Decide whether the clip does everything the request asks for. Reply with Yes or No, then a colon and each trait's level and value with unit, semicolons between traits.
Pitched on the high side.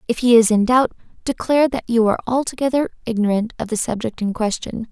Yes: high, 235 Hz